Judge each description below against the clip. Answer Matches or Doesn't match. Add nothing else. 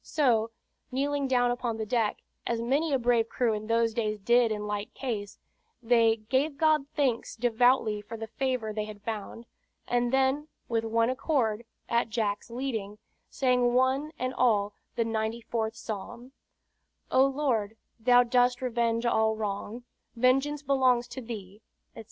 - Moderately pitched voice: Doesn't match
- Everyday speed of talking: Matches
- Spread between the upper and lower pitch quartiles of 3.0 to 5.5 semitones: Doesn't match